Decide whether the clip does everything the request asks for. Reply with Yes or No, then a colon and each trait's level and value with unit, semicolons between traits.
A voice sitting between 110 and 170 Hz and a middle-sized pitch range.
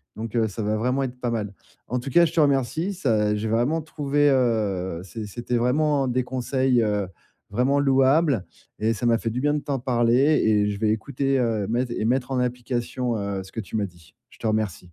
Yes: low, 120 Hz; average, 3.8 semitones